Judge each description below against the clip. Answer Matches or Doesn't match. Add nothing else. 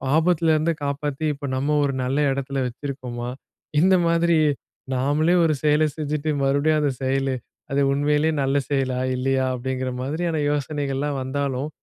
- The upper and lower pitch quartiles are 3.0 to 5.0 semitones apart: Doesn't match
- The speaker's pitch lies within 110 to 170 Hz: Matches